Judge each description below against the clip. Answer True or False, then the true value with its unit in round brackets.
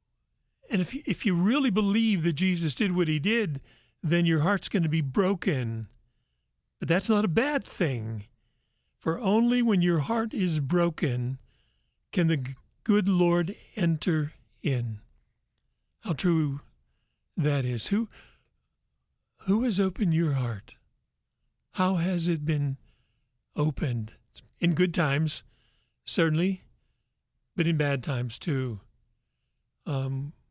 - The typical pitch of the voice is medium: True (165 Hz)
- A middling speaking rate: False (120 wpm)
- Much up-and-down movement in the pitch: True (6.3 semitones)